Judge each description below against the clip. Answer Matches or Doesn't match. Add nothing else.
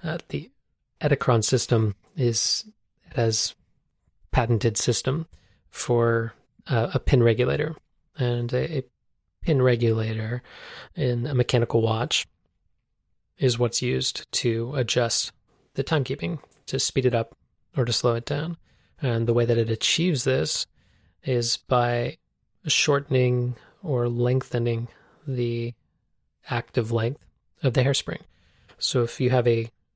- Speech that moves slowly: Matches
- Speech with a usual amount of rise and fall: Doesn't match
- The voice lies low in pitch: Matches